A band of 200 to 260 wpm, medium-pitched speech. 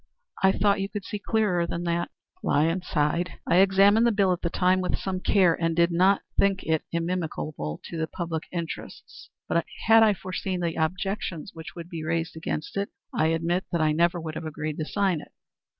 Yes: fast, 205 wpm; medium, 175 Hz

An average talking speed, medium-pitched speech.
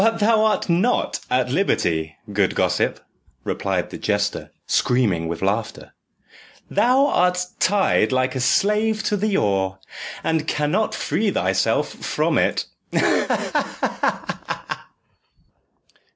No: slow, 115 wpm; medium, 150 Hz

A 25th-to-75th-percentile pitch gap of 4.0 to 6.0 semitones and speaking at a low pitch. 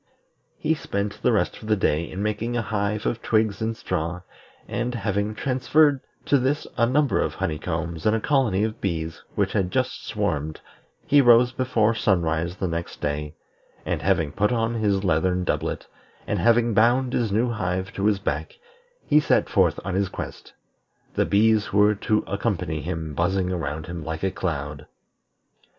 Yes: average, 5.1 semitones; low, 100 Hz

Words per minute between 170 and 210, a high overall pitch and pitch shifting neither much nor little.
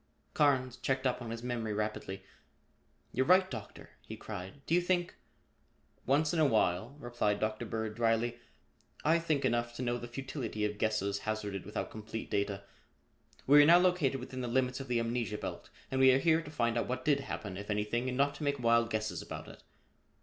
No: average, 200 wpm; low, 120 Hz; average, 4.0 semitones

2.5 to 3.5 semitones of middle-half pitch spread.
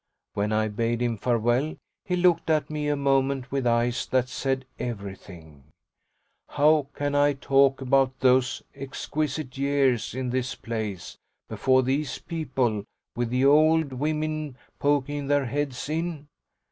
Yes: average, 3.1 semitones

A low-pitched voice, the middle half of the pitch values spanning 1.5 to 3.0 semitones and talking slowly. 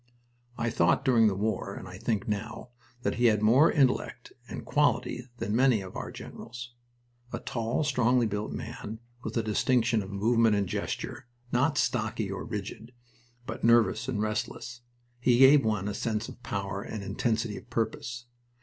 No: low, 115 Hz; narrow, 2.5 semitones; average, 170 wpm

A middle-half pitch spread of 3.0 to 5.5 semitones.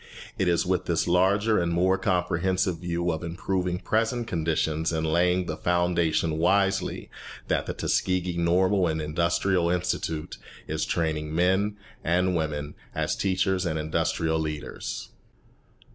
No: narrow, 2.4 semitones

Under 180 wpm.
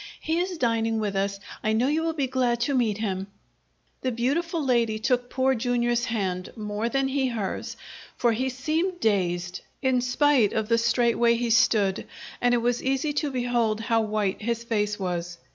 No: average, 185 wpm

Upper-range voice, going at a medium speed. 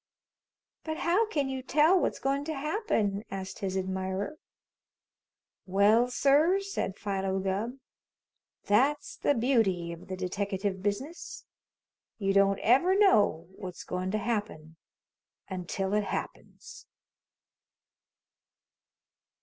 No: high, 205 Hz; slow, 110 wpm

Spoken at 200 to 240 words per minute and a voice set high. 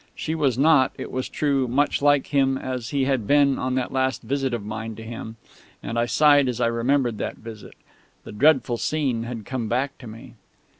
No: fast, 205 wpm; low, 130 Hz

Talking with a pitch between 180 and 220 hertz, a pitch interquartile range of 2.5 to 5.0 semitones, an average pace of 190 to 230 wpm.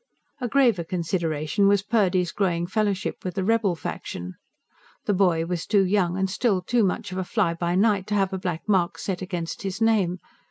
Yes: high, 190 Hz; average, 2.8 semitones; average, 195 wpm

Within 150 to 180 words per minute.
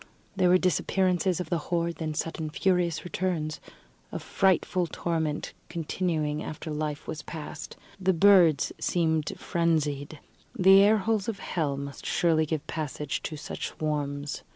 No: average, 140 wpm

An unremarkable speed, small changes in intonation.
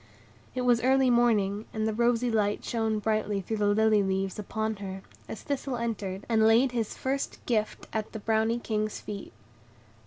Yes: average, 175 wpm; narrow, 2.2 semitones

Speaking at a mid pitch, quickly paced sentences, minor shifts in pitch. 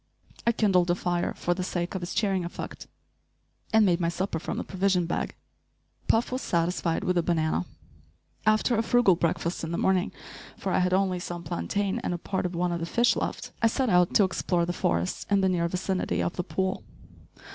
Yes: medium, 180 Hz; fast, 210 wpm; narrow, 2.2 semitones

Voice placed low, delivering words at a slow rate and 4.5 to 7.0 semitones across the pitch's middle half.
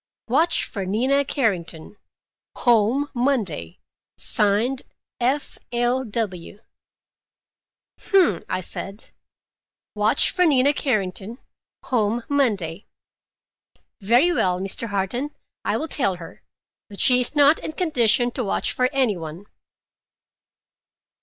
No: high, 235 Hz; slow, 105 wpm; wide, 5.5 semitones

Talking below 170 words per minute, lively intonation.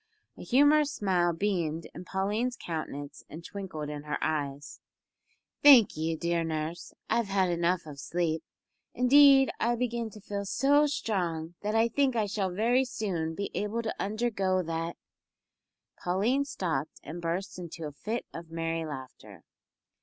Yes: average, 155 wpm; wide, 5.9 semitones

